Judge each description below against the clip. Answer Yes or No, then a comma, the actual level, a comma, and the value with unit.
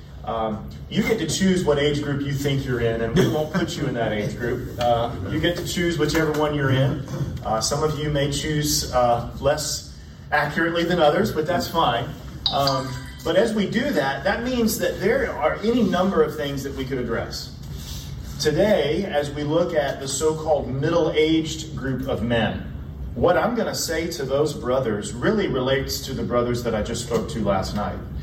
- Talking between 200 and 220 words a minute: Yes, fast, 205 wpm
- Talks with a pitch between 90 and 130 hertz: No, medium, 140 Hz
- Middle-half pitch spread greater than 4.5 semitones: Yes, average, 4.9 semitones